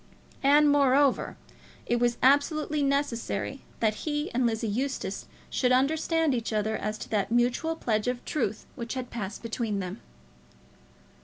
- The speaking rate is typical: Yes, average, 145 wpm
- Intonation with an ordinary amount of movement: Yes, average, 4.3 semitones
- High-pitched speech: Yes, very high, 250 Hz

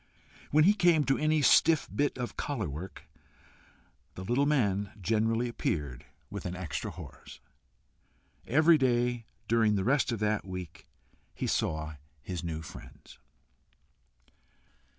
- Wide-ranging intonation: Yes, wide, 7.4 semitones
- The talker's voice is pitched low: Yes, low, 115 Hz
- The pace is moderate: No, slow, 130 wpm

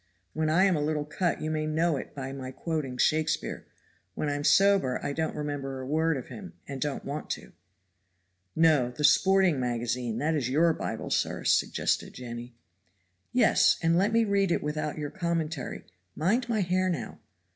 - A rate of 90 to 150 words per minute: No, average, 175 wpm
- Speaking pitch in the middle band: Yes, medium, 155 Hz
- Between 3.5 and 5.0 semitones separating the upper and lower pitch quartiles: Yes, average, 3.9 semitones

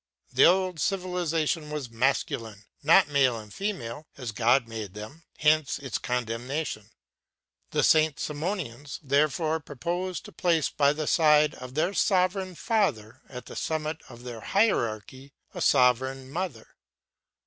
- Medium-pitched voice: Yes, medium, 145 Hz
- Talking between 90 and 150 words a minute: Yes, slow, 135 wpm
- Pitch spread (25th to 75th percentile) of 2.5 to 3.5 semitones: No, average, 5.1 semitones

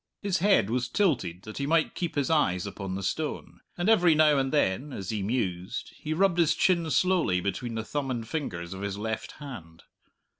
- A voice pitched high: No, low, 130 Hz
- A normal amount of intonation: No, wide, 8.5 semitones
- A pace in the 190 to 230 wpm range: Yes, average, 200 wpm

